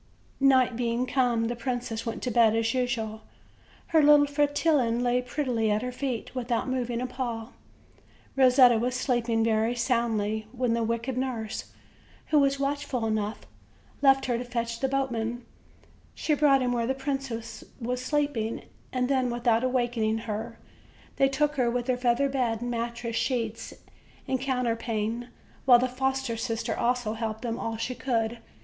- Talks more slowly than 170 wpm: Yes, average, 160 wpm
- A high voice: Yes, high, 245 Hz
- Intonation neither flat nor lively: No, narrow, 2.2 semitones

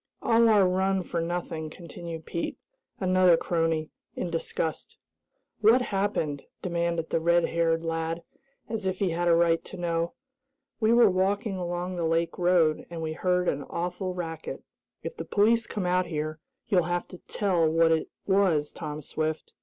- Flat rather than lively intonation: Yes, narrow, 2.3 semitones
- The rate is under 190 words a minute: Yes, average, 165 wpm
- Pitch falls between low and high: Yes, medium, 175 Hz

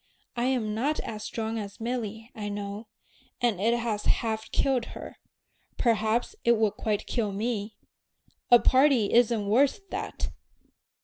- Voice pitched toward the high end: Yes, high, 225 Hz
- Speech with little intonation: Yes, narrow, 2.3 semitones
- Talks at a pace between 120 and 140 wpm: Yes, slow, 135 wpm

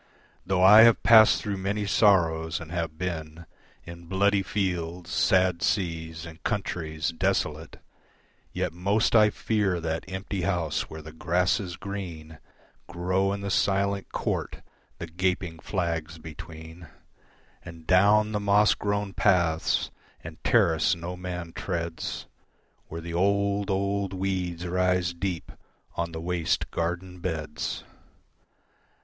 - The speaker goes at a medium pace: No, slow, 125 wpm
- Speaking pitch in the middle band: No, very low, 90 Hz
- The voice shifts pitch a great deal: No, average, 3.0 semitones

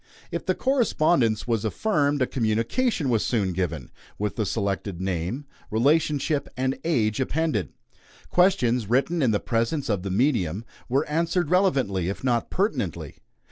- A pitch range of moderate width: No, wide, 6.9 semitones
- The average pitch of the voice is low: Yes, low, 120 Hz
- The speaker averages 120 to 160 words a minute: Yes, average, 140 wpm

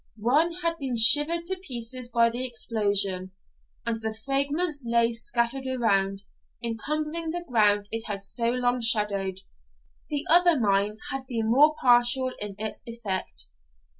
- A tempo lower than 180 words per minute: Yes, average, 140 wpm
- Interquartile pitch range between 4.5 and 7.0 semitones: No, average, 4.1 semitones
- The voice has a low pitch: No, high, 235 Hz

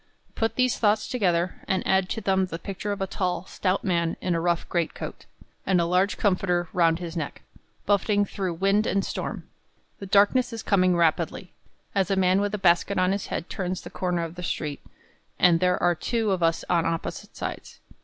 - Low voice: No, medium, 185 Hz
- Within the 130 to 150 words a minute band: No, fast, 205 wpm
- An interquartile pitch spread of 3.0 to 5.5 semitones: No, narrow, 2.5 semitones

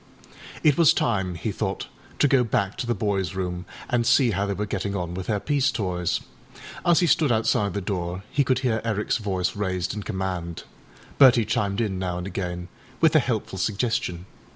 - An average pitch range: Yes, average, 4.3 semitones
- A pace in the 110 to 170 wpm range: No, average, 195 wpm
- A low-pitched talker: Yes, low, 100 Hz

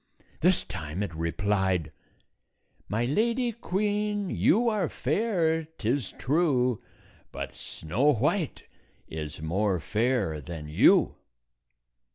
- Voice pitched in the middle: No, low, 125 Hz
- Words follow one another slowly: Yes, slow, 105 wpm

